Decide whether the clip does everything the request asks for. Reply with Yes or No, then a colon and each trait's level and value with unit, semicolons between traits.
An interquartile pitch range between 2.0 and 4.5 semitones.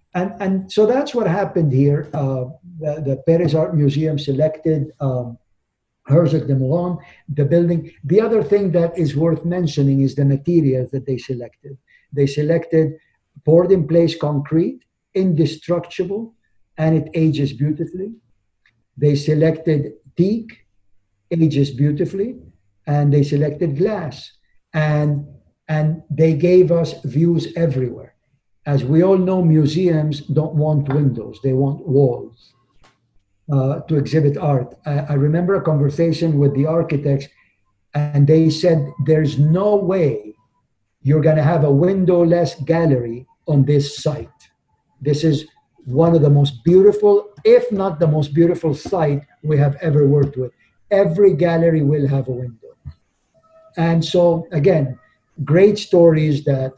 Yes: average, 3.4 semitones